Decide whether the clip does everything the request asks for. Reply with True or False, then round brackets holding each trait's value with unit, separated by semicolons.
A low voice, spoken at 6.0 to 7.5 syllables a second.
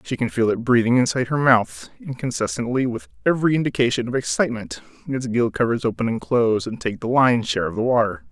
True (120 Hz; 6.3 syllables/s)